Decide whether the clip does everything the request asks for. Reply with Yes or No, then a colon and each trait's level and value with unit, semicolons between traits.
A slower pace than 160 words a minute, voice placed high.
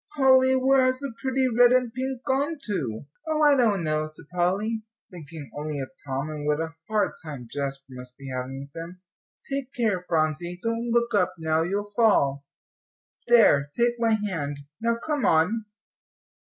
No: average, 170 wpm; high, 200 Hz